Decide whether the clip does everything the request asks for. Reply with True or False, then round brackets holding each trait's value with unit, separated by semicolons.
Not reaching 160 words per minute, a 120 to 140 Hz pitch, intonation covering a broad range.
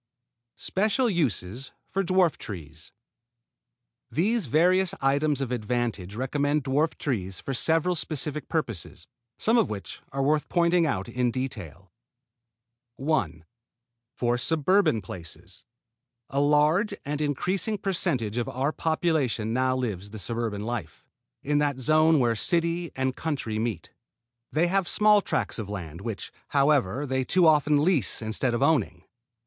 True (135 wpm; 135 Hz; 5.9 semitones)